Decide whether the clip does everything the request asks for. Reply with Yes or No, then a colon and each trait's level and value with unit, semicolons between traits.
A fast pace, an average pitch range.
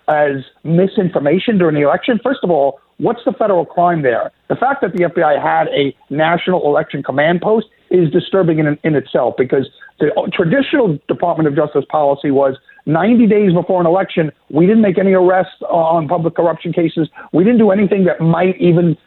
No: average, 185 wpm; average, 3.8 semitones